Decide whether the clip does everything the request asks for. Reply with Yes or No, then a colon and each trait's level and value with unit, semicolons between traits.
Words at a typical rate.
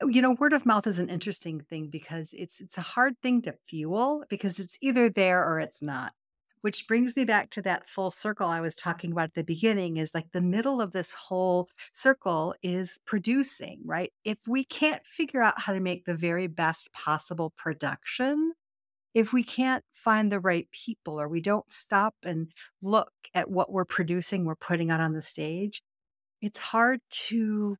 Yes: average, 190 wpm